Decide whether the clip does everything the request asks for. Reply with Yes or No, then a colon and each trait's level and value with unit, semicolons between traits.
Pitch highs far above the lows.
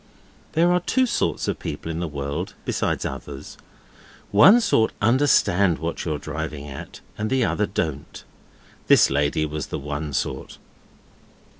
Yes: wide, 7.4 semitones